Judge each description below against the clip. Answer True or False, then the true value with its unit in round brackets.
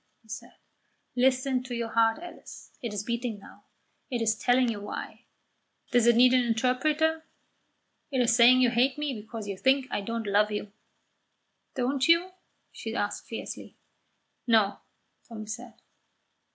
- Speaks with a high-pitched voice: True (240 Hz)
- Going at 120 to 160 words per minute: True (150 wpm)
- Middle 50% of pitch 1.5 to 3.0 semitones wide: True (2.6 semitones)